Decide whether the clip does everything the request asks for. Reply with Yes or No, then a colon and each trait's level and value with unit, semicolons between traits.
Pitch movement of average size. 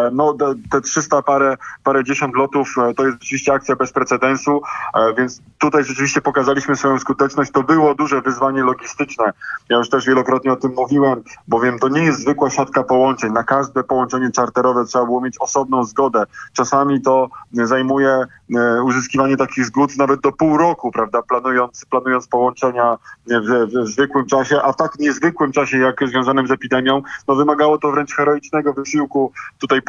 No: narrow, 1.7 semitones